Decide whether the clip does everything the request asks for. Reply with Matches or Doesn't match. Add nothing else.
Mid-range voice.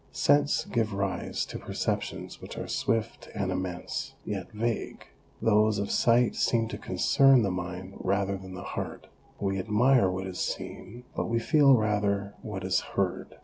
Doesn't match